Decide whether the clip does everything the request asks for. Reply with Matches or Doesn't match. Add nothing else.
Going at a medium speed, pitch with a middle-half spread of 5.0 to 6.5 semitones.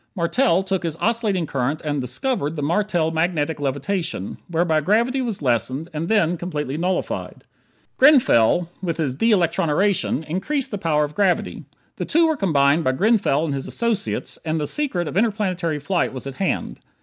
Matches